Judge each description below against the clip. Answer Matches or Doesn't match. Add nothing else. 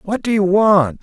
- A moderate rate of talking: Doesn't match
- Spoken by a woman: Doesn't match